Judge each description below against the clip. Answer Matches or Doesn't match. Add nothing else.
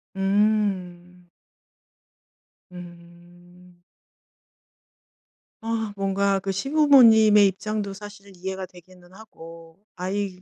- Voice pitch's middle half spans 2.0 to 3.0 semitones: Matches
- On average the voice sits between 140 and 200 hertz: Matches